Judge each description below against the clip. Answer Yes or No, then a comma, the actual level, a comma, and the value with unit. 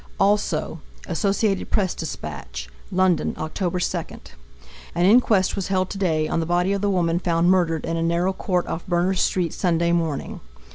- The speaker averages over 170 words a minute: No, average, 155 wpm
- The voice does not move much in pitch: Yes, narrow, 2.2 semitones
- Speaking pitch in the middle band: Yes, medium, 175 Hz